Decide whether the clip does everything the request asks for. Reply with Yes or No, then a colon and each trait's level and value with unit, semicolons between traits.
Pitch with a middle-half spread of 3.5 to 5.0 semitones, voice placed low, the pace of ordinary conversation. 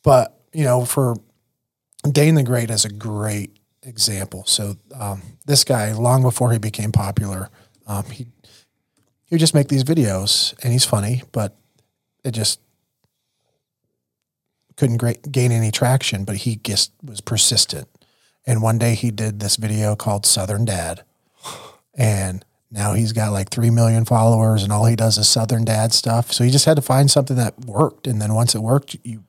No: average, 3.1 semitones; low, 115 Hz; average, 175 wpm